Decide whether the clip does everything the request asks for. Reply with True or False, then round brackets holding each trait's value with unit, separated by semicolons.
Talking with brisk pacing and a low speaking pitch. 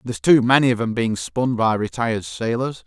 True (210 wpm; 120 Hz)